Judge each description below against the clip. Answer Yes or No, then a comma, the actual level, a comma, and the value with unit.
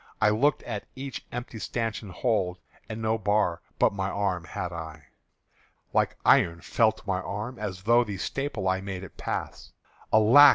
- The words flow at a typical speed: Yes, average, 165 wpm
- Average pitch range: Yes, average, 3.5 semitones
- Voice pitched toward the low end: Yes, low, 105 Hz